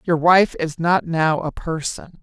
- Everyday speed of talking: Yes, average, 190 wpm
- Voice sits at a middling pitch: Yes, medium, 165 Hz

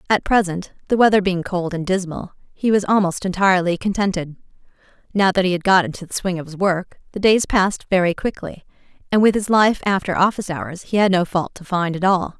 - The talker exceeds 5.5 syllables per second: Yes, 5.8 syllables/s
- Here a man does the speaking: No, female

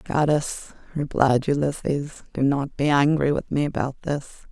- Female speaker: Yes, female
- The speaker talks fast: No, average, 145 wpm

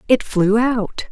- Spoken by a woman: Yes, female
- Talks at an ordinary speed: Yes, average, 160 wpm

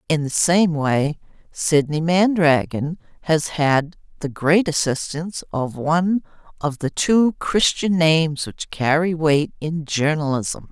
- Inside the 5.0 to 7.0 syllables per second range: No, 3.8 syllables/s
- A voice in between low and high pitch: Yes, medium, 160 Hz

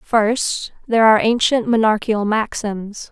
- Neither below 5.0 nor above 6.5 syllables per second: No, 4.4 syllables/s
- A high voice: Yes, high, 220 Hz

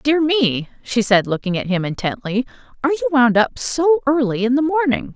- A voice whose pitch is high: Yes, very high, 250 Hz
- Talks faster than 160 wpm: Yes, average, 200 wpm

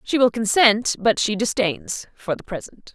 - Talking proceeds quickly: No, average, 165 wpm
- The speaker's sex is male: No, female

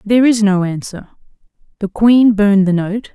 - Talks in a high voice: Yes, high, 210 Hz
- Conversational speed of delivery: Yes, average, 170 wpm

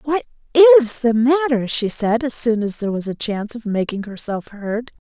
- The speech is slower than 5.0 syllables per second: No, 5.3 syllables/s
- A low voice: No, high, 235 Hz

